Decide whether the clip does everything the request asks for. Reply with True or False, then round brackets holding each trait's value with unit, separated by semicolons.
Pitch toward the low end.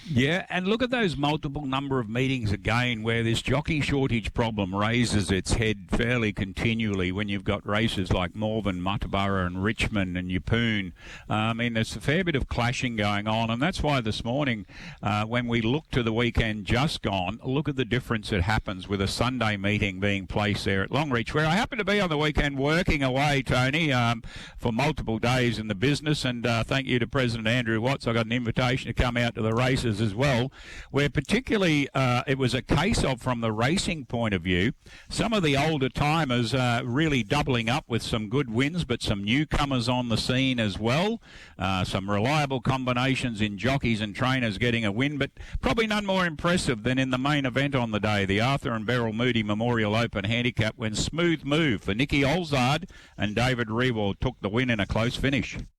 True (120 Hz)